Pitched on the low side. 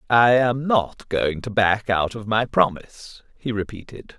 Yes: low, 110 Hz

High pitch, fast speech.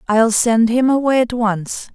No: high, 230 Hz; average, 185 wpm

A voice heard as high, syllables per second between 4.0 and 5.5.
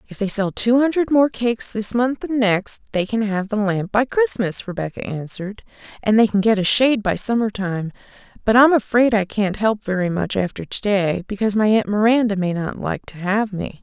Yes: high, 210 Hz; 5.2 syllables/s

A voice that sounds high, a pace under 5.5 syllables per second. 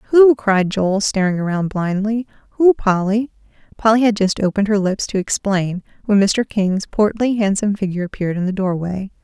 Yes: high, 205 Hz; 5.3 syllables/s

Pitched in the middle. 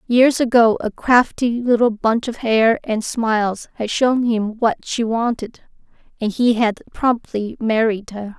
No: high, 230 Hz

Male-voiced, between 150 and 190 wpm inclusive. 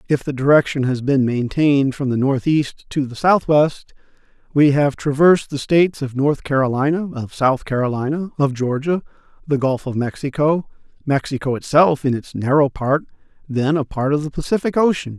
Yes: male; average, 165 wpm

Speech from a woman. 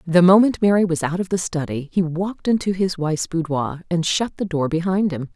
Yes: female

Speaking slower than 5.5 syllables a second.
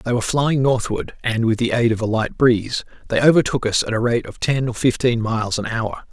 No: 5.6 syllables/s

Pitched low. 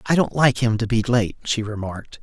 Yes: low, 115 Hz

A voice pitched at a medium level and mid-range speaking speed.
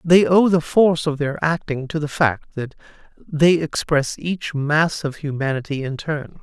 Yes: medium, 155 Hz; average, 175 wpm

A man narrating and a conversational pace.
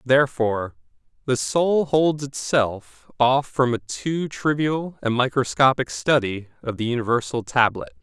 No: male; slow, 125 wpm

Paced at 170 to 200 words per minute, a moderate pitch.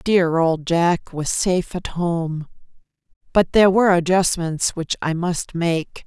No: average, 150 wpm; medium, 170 Hz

